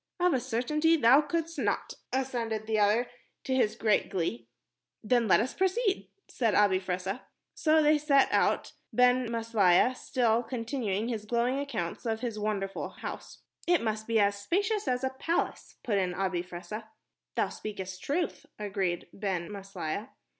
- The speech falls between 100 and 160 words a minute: Yes, average, 155 wpm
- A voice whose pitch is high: Yes, high, 230 Hz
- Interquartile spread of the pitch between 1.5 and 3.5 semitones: No, average, 4.7 semitones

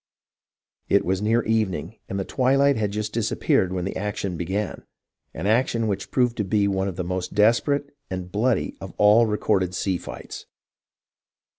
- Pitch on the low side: Yes, low, 105 Hz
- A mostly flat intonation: No, average, 3.3 semitones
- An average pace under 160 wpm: No, average, 170 wpm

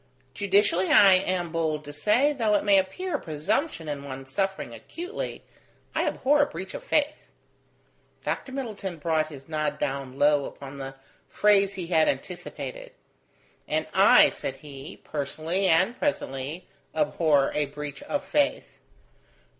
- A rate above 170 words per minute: No, average, 145 wpm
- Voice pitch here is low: No, medium, 170 Hz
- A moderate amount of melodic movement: No, wide, 6.2 semitones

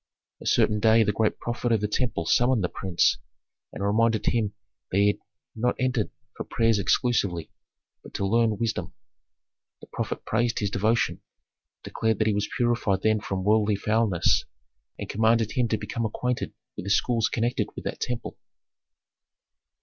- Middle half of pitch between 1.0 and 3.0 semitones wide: Yes, narrow, 2.4 semitones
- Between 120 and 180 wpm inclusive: Yes, average, 165 wpm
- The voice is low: Yes, low, 110 Hz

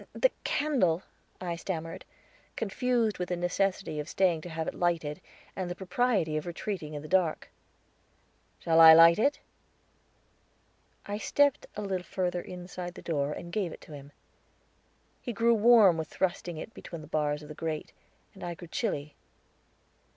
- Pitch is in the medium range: Yes, medium, 175 Hz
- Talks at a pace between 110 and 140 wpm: No, average, 165 wpm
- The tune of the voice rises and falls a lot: No, average, 3.6 semitones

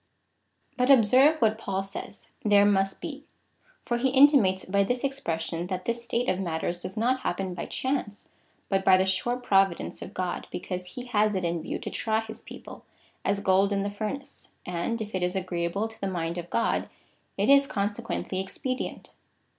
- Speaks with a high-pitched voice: Yes, high, 200 Hz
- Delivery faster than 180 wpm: Yes, average, 195 wpm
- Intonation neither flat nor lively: Yes, average, 4.3 semitones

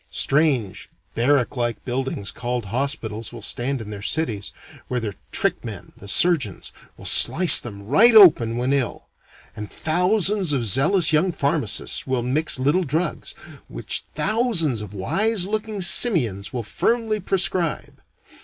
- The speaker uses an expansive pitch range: Yes, wide, 7.6 semitones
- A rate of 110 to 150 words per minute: Yes, average, 140 wpm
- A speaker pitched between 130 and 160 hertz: Yes, medium, 140 Hz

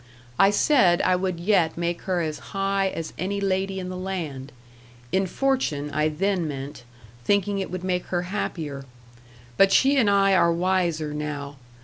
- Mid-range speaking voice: Yes, medium, 180 Hz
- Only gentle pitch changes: No, average, 3.7 semitones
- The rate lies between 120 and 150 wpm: No, average, 165 wpm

